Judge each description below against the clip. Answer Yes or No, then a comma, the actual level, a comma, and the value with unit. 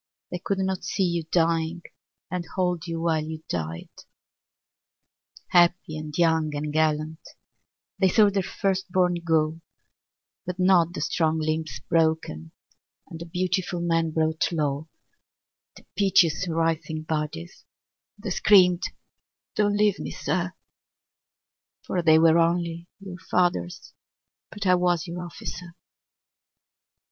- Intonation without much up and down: Yes, narrow, 2.2 semitones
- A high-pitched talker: No, medium, 170 Hz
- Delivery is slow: Yes, slow, 130 wpm